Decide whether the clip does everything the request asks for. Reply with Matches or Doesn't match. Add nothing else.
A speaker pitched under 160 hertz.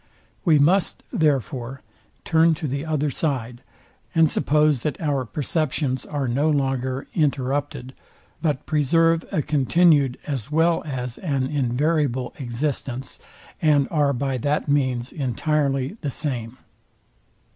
Matches